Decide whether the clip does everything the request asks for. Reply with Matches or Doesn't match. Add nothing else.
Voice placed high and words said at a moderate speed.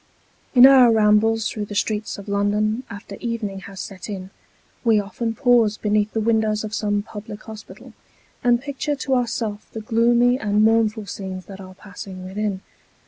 Matches